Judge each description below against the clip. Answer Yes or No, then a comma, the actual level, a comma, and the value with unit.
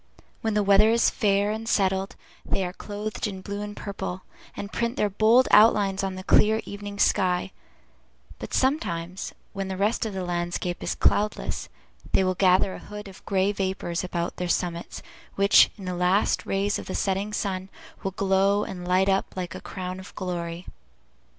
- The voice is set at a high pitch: Yes, high, 195 Hz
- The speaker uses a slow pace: No, average, 180 wpm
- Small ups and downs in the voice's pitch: Yes, narrow, 2.0 semitones